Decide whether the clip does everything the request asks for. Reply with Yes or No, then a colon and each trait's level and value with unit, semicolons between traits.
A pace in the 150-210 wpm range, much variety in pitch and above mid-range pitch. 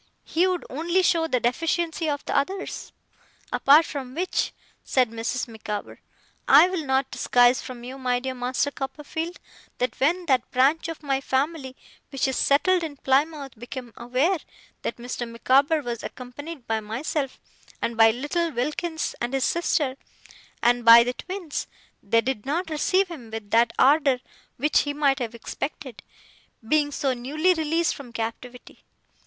No: average, 155 wpm; average, 4.4 semitones; very high, 270 Hz